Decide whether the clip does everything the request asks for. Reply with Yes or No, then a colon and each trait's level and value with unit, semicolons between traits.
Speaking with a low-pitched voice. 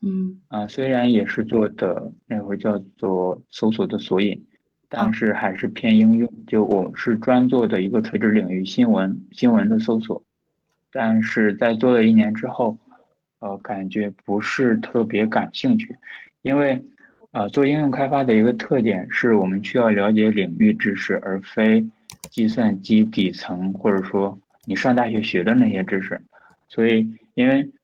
Yes: low, 120 Hz